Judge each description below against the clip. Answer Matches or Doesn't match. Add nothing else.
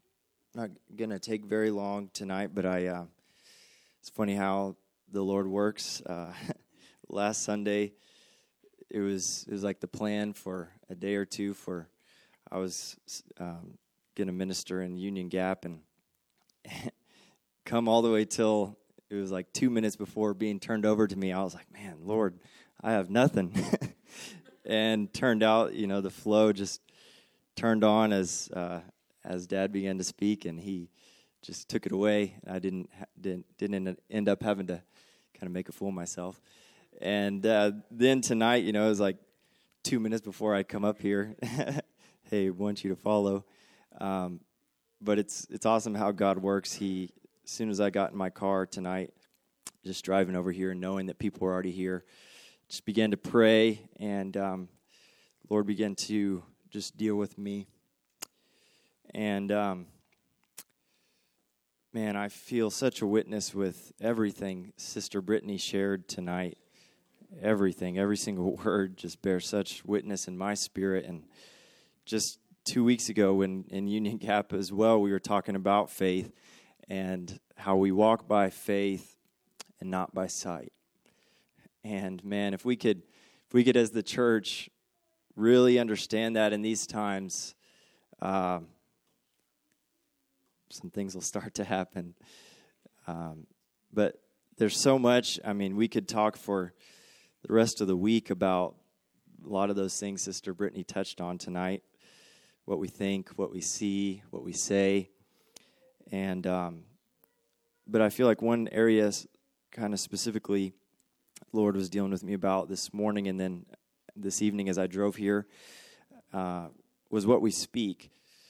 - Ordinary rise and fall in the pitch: Doesn't match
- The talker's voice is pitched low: Matches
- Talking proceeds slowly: Doesn't match